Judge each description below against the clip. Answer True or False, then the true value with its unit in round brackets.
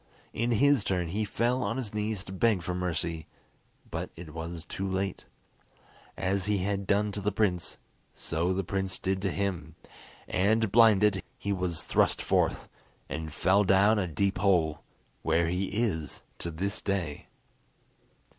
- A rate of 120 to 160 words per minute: True (155 wpm)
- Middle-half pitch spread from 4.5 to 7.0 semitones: False (2.9 semitones)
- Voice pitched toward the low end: True (95 Hz)